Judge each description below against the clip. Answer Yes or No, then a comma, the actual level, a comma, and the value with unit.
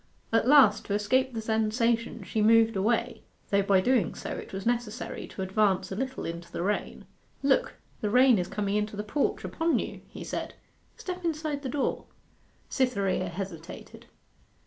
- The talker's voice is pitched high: Yes, high, 220 Hz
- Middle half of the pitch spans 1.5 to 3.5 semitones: No, average, 4.6 semitones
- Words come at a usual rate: Yes, average, 170 wpm